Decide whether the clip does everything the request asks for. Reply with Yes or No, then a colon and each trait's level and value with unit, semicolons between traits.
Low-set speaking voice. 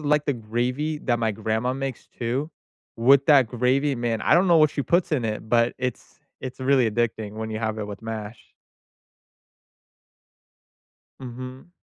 Yes: low, 125 Hz